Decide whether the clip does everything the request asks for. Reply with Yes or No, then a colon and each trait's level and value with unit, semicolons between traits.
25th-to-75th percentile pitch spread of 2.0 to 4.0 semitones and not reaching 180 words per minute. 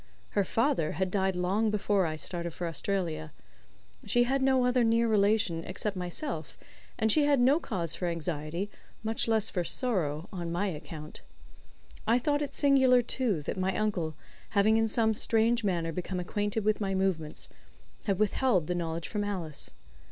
No: average, 4.8 semitones; average, 165 wpm